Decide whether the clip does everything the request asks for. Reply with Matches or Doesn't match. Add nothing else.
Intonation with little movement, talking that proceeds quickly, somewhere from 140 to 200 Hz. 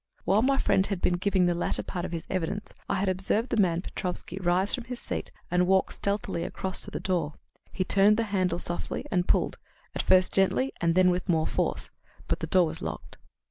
Matches